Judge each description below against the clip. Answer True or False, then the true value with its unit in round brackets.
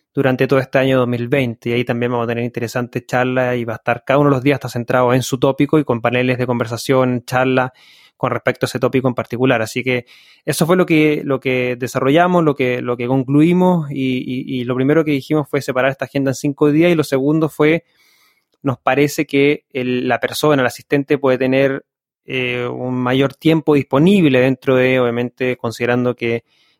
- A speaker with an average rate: False (205 wpm)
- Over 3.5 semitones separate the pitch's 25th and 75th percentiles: False (2.5 semitones)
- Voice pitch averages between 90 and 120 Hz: False (130 Hz)